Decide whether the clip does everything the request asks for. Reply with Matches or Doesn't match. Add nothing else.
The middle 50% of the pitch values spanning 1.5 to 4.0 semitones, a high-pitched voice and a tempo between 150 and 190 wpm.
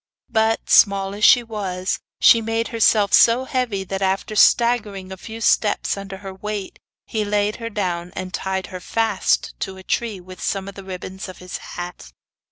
Matches